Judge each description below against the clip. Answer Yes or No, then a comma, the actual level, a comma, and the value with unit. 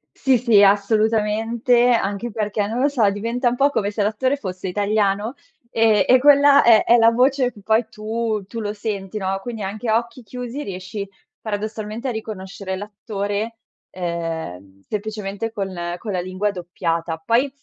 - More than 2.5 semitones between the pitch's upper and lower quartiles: Yes, average, 2.9 semitones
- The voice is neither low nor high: No, high, 215 Hz